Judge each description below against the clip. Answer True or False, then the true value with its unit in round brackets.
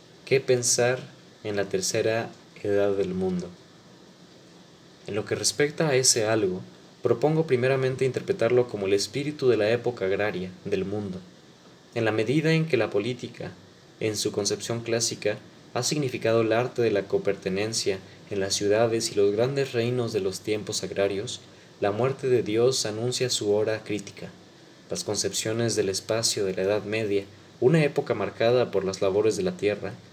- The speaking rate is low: False (160 wpm)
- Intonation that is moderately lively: True (3.8 semitones)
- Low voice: True (115 Hz)